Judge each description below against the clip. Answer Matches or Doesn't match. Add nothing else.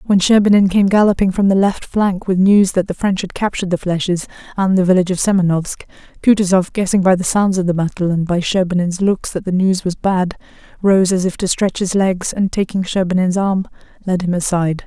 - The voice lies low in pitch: Doesn't match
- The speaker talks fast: Matches